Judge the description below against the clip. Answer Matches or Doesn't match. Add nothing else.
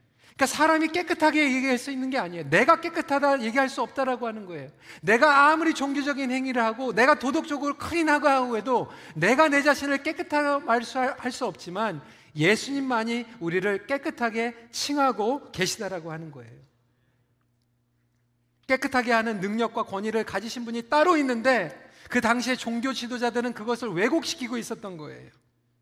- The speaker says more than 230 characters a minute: Matches